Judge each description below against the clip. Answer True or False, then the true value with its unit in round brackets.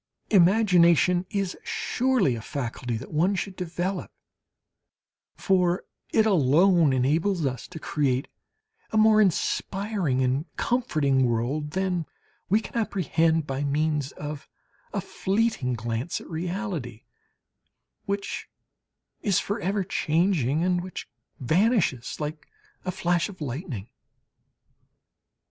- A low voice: False (170 Hz)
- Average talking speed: False (110 wpm)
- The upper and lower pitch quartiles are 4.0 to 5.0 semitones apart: False (5.6 semitones)